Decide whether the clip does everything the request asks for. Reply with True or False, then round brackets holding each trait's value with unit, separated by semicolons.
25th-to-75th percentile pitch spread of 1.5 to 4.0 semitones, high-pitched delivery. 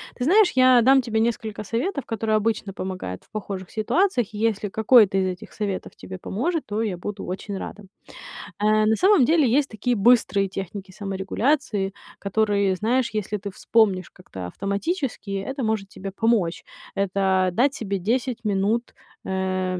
True (3.6 semitones; 210 Hz)